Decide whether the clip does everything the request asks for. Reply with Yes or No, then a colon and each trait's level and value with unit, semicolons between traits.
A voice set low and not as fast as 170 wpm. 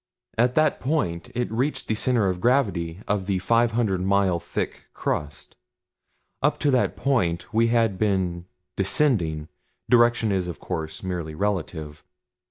Yes: low, 100 Hz; average, 145 wpm